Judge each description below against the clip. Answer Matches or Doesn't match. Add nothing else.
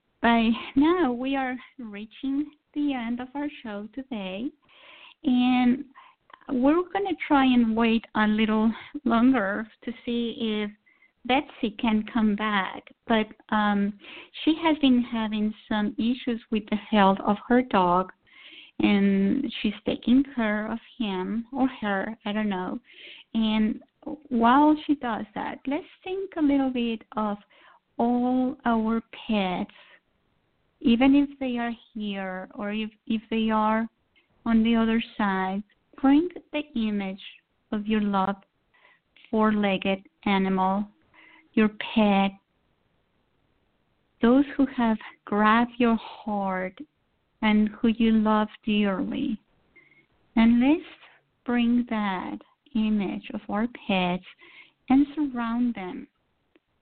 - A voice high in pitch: Matches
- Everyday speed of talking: Doesn't match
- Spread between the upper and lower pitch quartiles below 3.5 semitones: Doesn't match